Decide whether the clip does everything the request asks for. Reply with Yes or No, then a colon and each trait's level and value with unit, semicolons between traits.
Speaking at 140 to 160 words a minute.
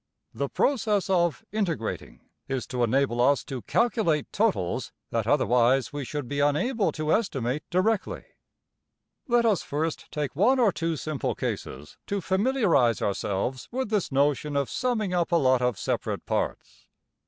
Yes: average, 150 wpm